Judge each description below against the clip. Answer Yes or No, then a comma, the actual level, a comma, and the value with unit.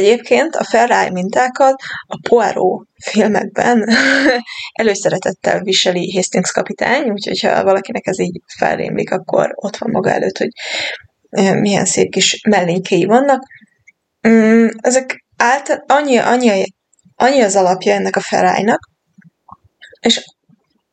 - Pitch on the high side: Yes, high, 220 Hz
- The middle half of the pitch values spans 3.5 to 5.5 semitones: Yes, average, 4.5 semitones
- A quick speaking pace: No, average, 110 wpm